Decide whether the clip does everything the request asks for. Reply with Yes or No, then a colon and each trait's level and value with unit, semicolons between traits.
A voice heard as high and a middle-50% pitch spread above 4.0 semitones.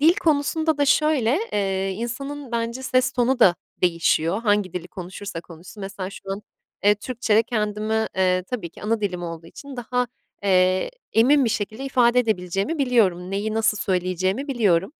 Yes: high, 215 Hz; average, 5.0 semitones